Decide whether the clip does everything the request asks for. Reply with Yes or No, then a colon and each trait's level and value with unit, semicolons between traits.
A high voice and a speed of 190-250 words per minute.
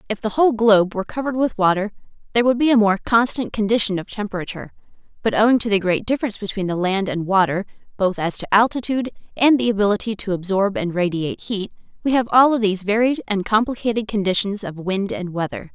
Yes: high, 210 Hz; average, 200 wpm